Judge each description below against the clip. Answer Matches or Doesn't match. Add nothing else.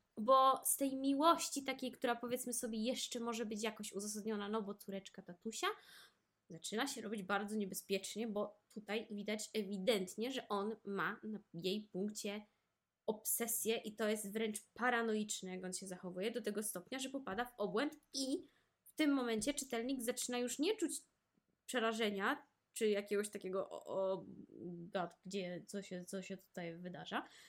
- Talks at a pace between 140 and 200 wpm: Matches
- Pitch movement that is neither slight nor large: Matches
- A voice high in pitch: Matches